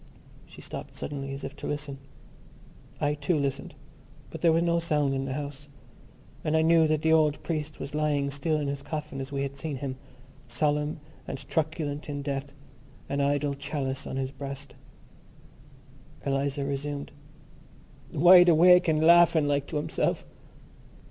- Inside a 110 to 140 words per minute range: No, average, 160 wpm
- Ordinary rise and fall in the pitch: No, narrow, 1.9 semitones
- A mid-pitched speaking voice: Yes, medium, 145 Hz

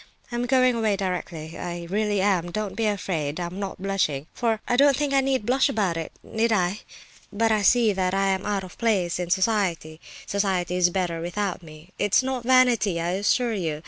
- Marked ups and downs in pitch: No, average, 4.2 semitones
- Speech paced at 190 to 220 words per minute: Yes, average, 195 wpm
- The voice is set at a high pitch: Yes, high, 195 Hz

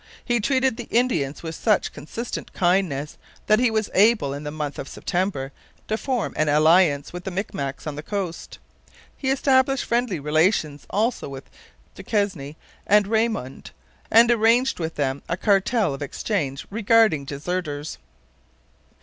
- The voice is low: No, medium, 185 Hz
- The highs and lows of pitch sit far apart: Yes, wide, 7.3 semitones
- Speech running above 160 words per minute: No, average, 145 wpm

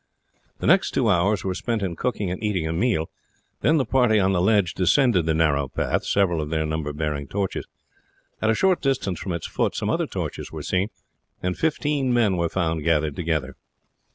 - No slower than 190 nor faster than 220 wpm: Yes, average, 200 wpm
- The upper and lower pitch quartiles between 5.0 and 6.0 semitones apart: Yes, wide, 5.4 semitones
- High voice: No, very low, 90 Hz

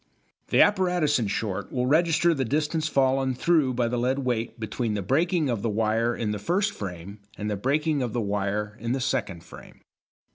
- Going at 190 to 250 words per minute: Yes, average, 195 wpm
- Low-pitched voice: Yes, low, 125 Hz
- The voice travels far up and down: Yes, wide, 6.1 semitones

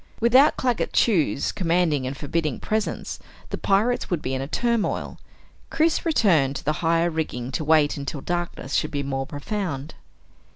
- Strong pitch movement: Yes, wide, 6.9 semitones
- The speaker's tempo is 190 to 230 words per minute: No, average, 160 wpm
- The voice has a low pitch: No, medium, 165 Hz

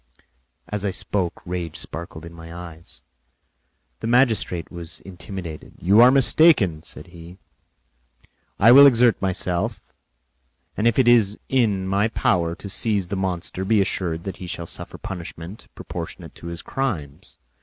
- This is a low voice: Yes, very low, 95 Hz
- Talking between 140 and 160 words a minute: Yes, average, 145 wpm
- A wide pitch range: No, average, 4.5 semitones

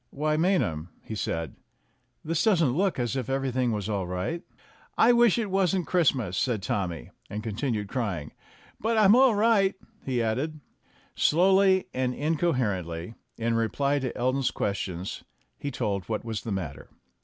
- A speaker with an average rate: Yes, average, 155 wpm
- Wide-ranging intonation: Yes, wide, 8.8 semitones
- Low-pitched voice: Yes, low, 130 Hz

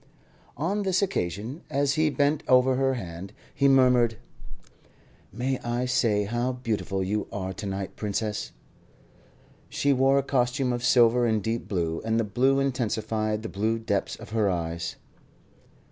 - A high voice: No, low, 120 Hz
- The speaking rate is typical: Yes, average, 150 wpm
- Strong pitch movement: No, average, 4.3 semitones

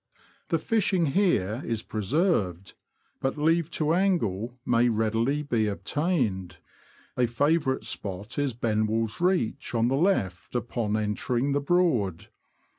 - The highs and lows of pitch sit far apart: Yes, wide, 6.5 semitones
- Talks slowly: Yes, slow, 125 wpm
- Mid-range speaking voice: No, low, 120 Hz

